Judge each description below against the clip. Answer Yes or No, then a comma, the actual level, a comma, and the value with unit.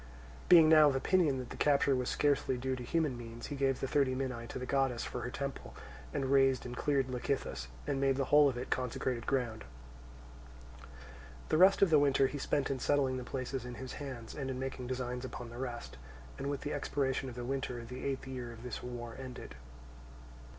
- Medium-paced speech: No, fast, 210 wpm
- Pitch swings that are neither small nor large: No, narrow, 2.0 semitones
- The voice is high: No, low, 130 Hz